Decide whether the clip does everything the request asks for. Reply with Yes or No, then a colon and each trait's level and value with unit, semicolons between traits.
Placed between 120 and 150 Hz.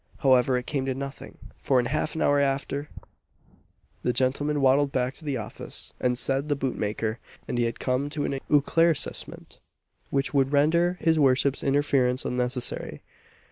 Yes: low, 135 Hz